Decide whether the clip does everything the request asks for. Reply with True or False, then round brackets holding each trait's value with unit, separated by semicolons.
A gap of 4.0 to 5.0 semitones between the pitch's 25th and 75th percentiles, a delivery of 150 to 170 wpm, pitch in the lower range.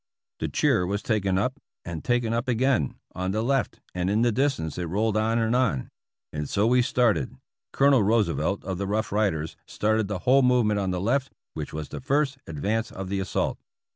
False (4.6 semitones; 205 wpm; 110 Hz)